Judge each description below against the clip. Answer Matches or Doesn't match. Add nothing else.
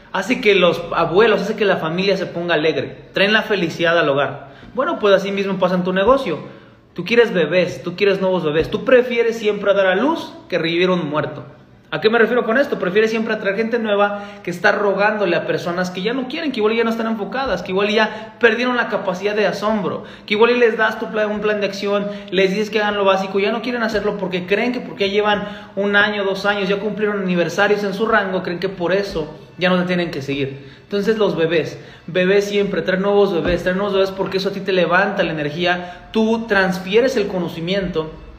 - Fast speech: Matches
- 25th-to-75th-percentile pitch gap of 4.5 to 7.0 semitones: Doesn't match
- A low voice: Doesn't match